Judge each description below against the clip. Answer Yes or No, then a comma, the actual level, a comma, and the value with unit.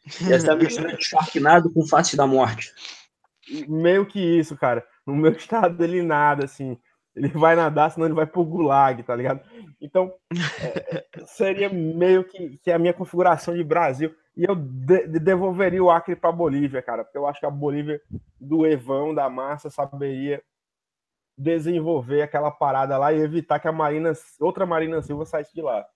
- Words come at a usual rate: Yes, average, 160 wpm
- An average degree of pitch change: Yes, average, 3.0 semitones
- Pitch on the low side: No, medium, 160 Hz